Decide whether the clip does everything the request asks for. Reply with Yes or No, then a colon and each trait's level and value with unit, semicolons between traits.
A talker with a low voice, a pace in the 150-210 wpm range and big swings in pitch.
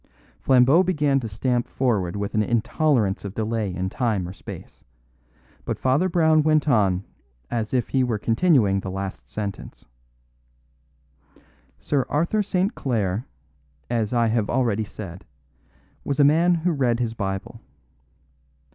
No: low, 120 Hz; average, 140 wpm; wide, 5.9 semitones